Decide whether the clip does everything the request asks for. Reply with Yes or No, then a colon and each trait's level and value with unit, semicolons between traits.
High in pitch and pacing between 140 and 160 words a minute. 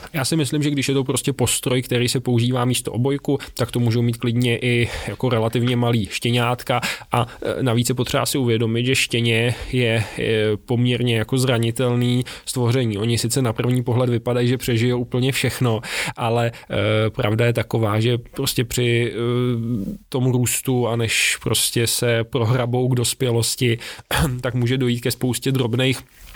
No: low, 120 Hz; average, 155 wpm